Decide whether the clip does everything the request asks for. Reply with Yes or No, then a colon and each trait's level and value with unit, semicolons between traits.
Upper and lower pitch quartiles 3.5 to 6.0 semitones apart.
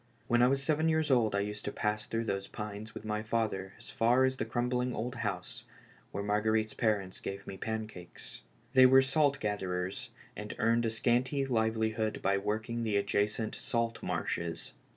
No: average, 2.9 semitones